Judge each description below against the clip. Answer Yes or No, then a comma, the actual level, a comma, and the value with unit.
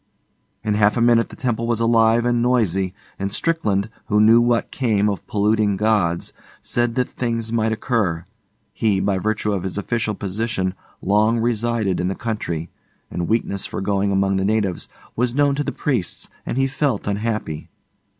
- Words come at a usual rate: Yes, average, 170 wpm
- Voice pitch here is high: No, low, 110 Hz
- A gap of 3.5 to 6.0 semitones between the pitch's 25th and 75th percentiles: No, average, 3.0 semitones